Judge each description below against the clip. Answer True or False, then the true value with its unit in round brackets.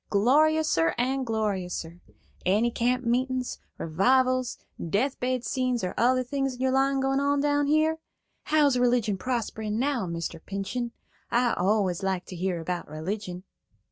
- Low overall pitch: False (240 Hz)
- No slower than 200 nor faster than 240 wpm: False (140 wpm)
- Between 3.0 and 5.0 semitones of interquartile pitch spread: False (5.5 semitones)